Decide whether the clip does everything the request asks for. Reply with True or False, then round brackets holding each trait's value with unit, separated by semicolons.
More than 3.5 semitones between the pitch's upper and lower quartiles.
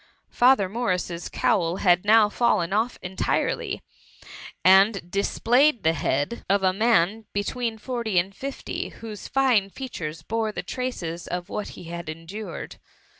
True (4.7 semitones)